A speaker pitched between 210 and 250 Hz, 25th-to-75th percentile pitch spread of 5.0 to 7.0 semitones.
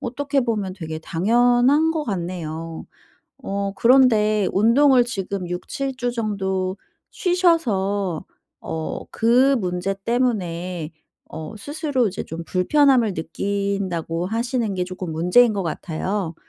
No: high, 200 Hz; wide, 5.4 semitones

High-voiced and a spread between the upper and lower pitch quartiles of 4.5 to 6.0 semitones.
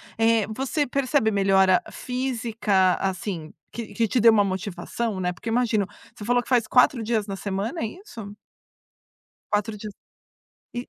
No: high, 220 Hz; average, 3.5 semitones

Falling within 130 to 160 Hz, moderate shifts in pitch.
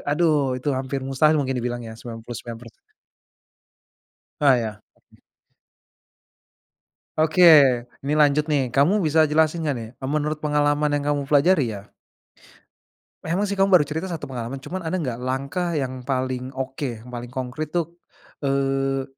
Yes: medium, 140 Hz; average, 3.3 semitones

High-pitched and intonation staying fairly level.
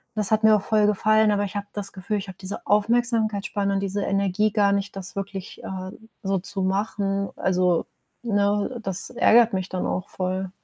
Yes: high, 200 Hz; narrow, 1.8 semitones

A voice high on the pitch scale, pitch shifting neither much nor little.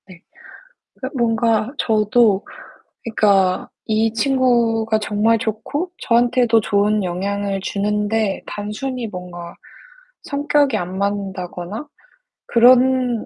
Yes: high, 220 Hz; average, 3.2 semitones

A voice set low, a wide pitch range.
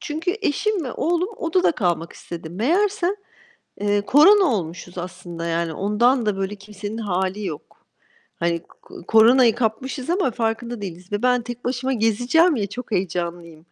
No: high, 220 Hz; wide, 6.3 semitones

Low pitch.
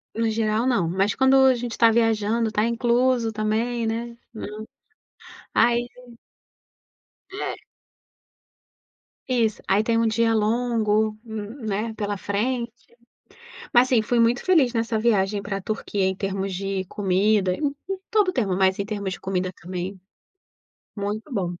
No: high, 220 Hz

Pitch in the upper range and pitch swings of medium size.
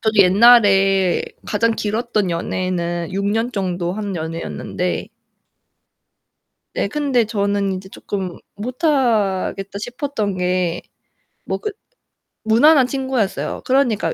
Yes: high, 205 Hz; average, 4.3 semitones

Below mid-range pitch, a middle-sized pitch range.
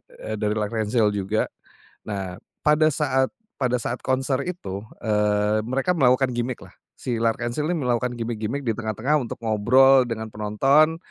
Yes: low, 120 Hz; average, 3.6 semitones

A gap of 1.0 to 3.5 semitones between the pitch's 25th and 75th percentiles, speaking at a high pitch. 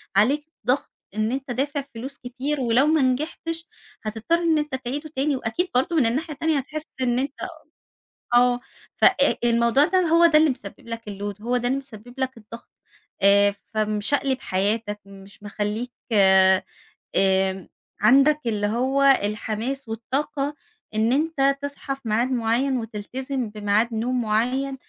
No: average, 4.4 semitones; very high, 250 Hz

